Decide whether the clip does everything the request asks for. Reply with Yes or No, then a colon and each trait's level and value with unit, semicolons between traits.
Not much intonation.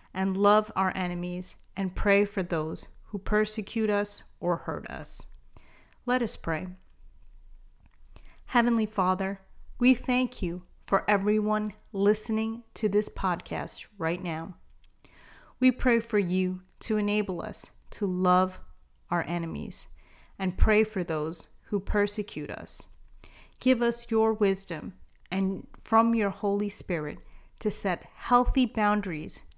No: average, 3.3 semitones